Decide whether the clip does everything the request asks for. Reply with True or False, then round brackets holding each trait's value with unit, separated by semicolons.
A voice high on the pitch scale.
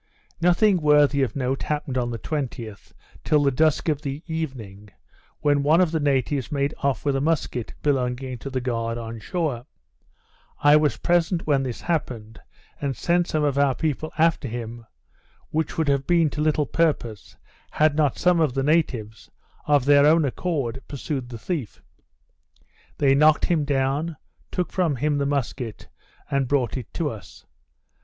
False (140 Hz)